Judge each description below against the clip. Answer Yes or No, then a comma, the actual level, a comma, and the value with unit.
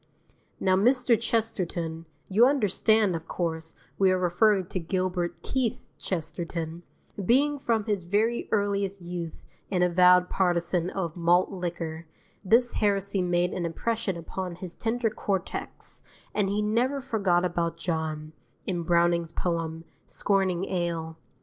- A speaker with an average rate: No, slow, 130 wpm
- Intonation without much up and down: No, average, 3.4 semitones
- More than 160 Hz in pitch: Yes, medium, 185 Hz